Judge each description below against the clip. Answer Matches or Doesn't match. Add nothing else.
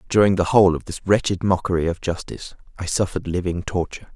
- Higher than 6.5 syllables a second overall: Matches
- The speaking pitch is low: Matches